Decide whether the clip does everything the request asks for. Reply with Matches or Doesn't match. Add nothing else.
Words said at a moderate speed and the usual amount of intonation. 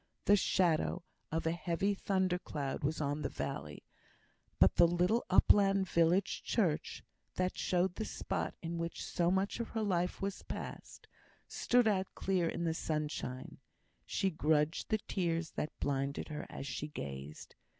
Matches